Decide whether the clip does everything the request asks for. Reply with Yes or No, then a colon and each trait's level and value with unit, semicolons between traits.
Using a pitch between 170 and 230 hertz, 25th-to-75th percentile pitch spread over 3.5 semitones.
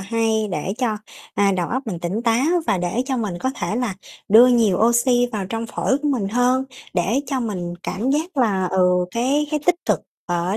Yes: high, 225 Hz; average, 4.8 semitones